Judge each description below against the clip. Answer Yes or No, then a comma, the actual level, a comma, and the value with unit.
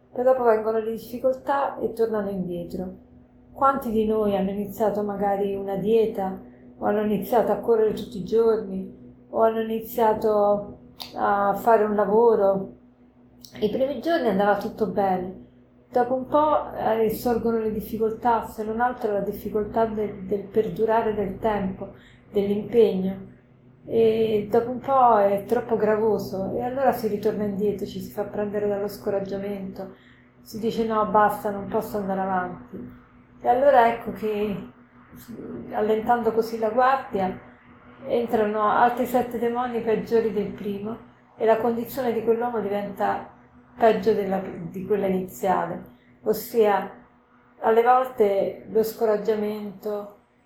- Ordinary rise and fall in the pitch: No, narrow, 2.1 semitones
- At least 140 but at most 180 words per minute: No, average, 130 wpm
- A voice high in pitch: Yes, high, 215 Hz